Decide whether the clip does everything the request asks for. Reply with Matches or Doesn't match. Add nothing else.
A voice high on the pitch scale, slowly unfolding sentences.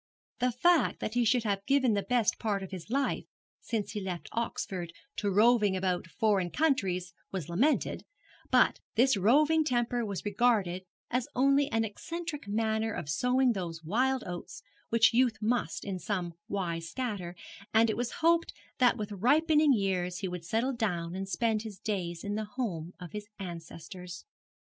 Doesn't match